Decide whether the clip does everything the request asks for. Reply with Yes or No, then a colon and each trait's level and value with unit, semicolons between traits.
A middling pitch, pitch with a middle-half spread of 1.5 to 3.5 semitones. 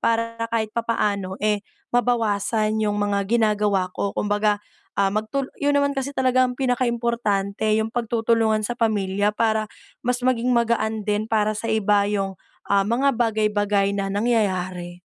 No: high, 215 Hz; narrow, 2.4 semitones